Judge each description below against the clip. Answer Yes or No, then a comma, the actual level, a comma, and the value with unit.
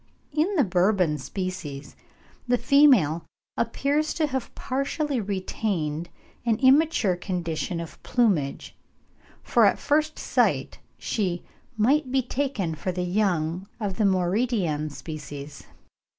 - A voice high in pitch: Yes, high, 195 Hz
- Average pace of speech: No, slow, 115 wpm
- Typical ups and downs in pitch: No, wide, 7.4 semitones